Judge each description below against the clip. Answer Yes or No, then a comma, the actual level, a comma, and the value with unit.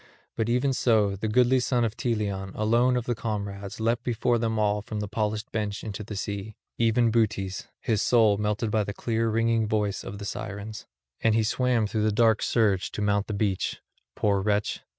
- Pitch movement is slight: Yes, narrow, 2.0 semitones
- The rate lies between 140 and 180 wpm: No, average, 195 wpm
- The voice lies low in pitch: Yes, low, 110 Hz